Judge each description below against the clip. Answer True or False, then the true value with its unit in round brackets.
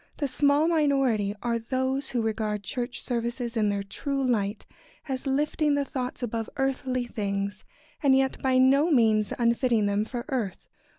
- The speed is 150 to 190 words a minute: True (165 wpm)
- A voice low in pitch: False (245 Hz)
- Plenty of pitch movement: False (3.7 semitones)